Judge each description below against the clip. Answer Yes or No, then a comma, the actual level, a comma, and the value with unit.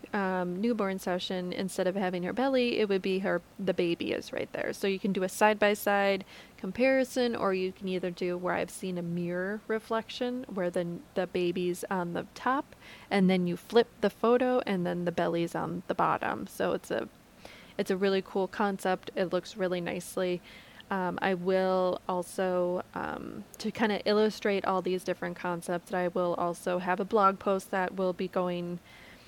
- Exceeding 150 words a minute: Yes, average, 190 wpm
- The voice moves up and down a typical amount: No, narrow, 2.2 semitones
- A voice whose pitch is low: No, high, 190 Hz